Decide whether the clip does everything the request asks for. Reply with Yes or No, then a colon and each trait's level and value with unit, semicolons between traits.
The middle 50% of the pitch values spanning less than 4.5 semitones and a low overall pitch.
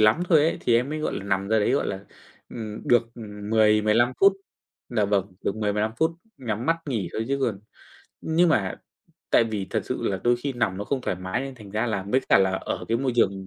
Yes: average, 3.8 semitones; low, 110 Hz